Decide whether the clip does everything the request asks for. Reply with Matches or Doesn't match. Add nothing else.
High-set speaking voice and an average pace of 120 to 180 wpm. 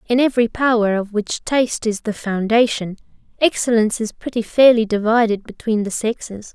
Matches